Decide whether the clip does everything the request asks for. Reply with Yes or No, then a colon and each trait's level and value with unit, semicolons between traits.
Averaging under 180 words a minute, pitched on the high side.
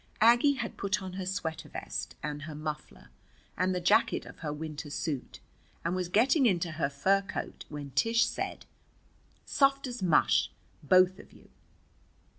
No: average, 160 wpm; medium, 180 Hz